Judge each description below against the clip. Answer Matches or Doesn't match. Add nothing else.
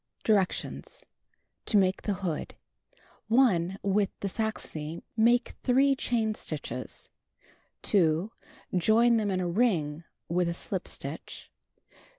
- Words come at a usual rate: Doesn't match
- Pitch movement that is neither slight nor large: Matches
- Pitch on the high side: Matches